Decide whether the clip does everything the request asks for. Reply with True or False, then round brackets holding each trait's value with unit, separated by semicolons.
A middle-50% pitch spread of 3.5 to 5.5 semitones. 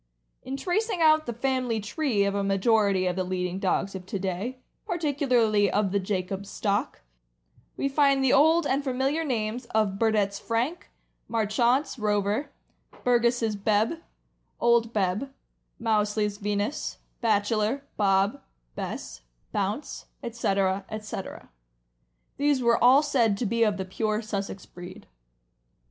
True (4.5 semitones)